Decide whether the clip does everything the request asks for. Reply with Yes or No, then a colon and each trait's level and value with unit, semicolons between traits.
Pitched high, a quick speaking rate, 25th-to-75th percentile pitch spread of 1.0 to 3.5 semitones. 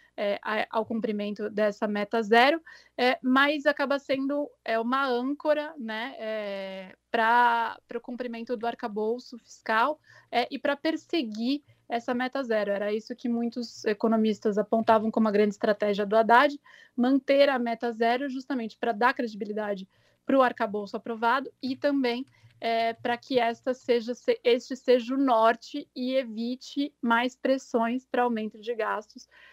No: high, 240 Hz; average, 145 wpm; average, 3.0 semitones